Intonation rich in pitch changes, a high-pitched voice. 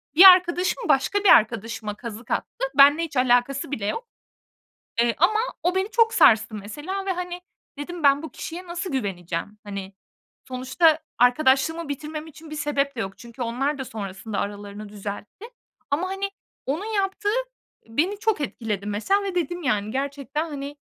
Yes: wide, 7.8 semitones; very high, 280 Hz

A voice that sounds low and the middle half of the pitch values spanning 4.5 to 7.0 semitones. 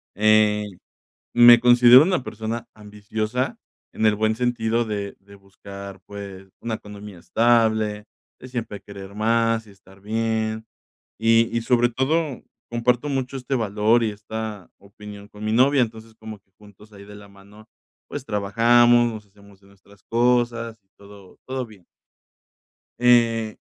No: low, 110 Hz; narrow, 2.6 semitones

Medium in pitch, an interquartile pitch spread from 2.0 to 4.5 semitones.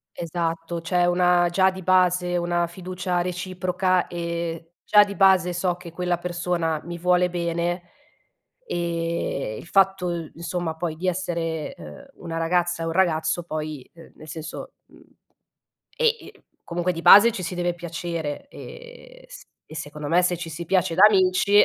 No: medium, 175 Hz; narrow, 1.6 semitones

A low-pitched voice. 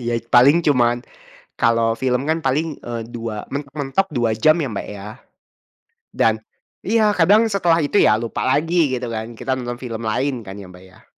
Yes: low, 125 Hz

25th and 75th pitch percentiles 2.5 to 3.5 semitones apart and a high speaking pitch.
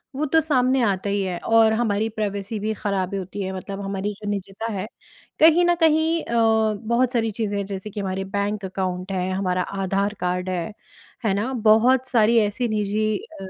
Yes: average, 2.9 semitones; high, 210 Hz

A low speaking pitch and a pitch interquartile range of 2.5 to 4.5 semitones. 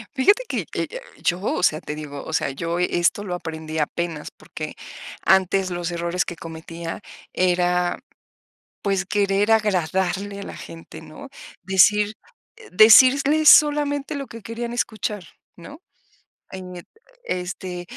No: medium, 185 Hz; average, 4.1 semitones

